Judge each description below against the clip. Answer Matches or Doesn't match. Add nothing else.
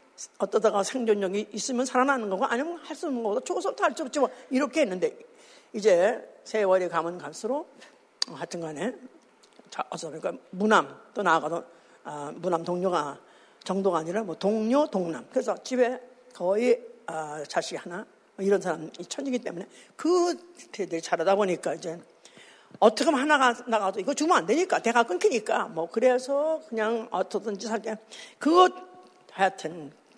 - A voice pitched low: Doesn't match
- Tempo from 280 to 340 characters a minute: Matches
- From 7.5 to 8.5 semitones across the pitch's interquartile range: Matches